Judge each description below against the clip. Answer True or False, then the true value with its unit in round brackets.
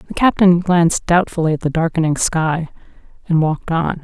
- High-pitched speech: False (165 Hz)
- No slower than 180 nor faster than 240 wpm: False (165 wpm)